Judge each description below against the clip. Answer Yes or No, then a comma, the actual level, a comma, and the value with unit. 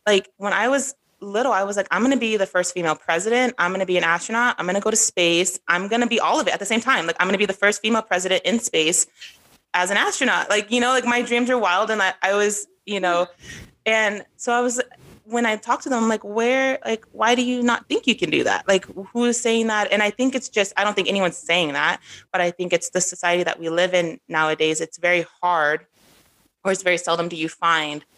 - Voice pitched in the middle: No, high, 200 Hz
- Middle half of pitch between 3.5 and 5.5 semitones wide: Yes, average, 4.8 semitones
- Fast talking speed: Yes, fast, 260 wpm